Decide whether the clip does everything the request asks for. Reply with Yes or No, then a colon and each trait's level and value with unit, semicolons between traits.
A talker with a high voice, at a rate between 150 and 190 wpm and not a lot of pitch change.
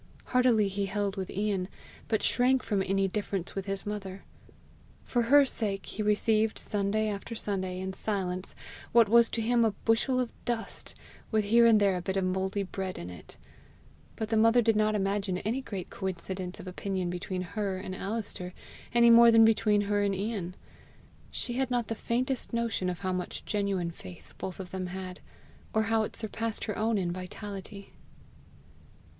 No: high, 205 Hz; average, 175 wpm; average, 3.1 semitones